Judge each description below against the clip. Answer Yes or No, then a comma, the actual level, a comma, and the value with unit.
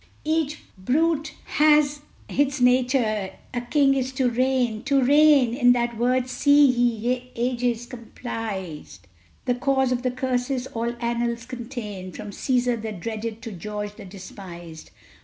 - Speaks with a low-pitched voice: No, high, 245 Hz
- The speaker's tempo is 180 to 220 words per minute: No, average, 140 wpm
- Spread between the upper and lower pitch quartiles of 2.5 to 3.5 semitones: Yes, average, 2.8 semitones